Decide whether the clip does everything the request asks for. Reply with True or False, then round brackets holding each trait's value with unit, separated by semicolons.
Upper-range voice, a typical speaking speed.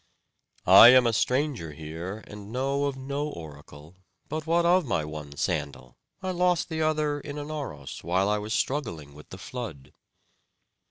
False (120 Hz; 160 wpm)